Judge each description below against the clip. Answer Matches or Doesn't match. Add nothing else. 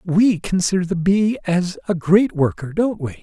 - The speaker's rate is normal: Matches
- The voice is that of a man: Matches